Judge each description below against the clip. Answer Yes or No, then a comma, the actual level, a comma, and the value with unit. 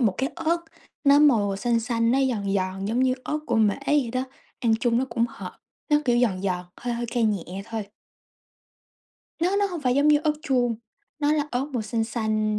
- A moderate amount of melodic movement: Yes, average, 4.4 semitones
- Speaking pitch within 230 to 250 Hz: Yes, high, 240 Hz